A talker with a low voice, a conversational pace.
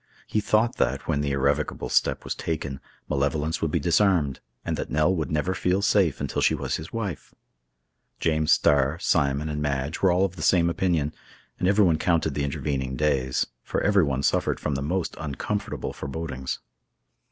Yes: very low, 80 Hz; average, 175 wpm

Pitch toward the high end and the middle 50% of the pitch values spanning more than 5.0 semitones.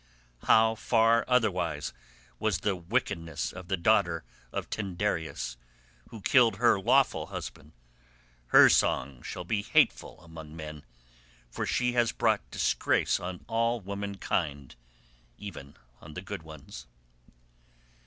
No: very low, 95 Hz; wide, 5.4 semitones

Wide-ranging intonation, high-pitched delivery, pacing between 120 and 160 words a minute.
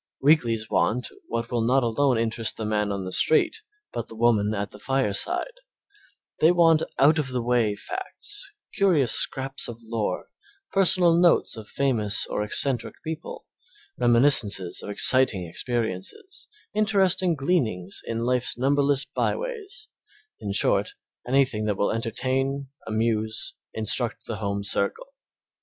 No: wide, 6.1 semitones; low, 125 Hz; slow, 135 wpm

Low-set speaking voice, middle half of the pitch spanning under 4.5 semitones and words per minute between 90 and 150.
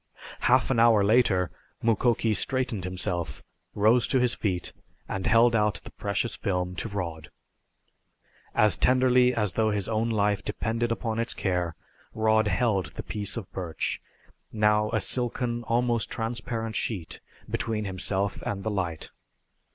Yes: low, 110 Hz; average, 3.1 semitones; average, 145 wpm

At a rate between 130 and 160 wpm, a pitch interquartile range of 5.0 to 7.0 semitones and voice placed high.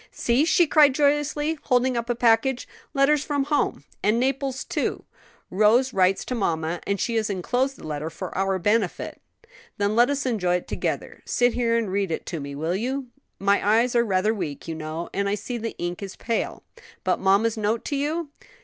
No: average, 195 wpm; wide, 5.5 semitones; high, 225 Hz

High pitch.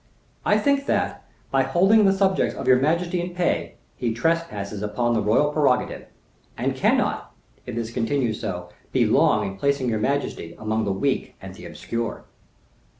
No: low, 130 Hz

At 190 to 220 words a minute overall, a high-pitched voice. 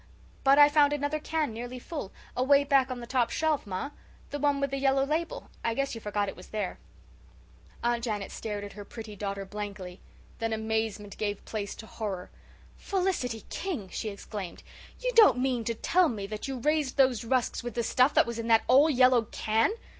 Yes: average, 200 wpm; high, 240 Hz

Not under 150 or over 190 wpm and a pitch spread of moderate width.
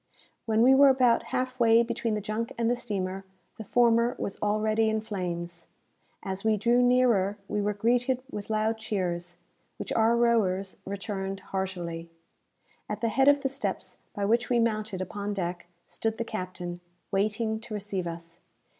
Yes: average, 165 wpm; average, 3.4 semitones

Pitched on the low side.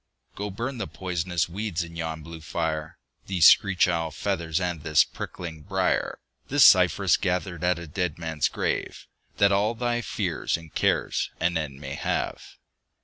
Yes: very low, 85 Hz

